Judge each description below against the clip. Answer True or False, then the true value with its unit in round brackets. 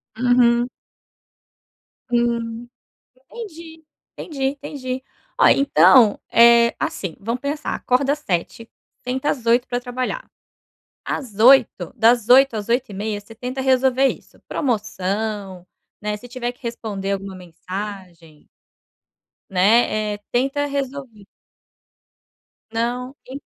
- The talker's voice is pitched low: False (235 Hz)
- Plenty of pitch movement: False (4.0 semitones)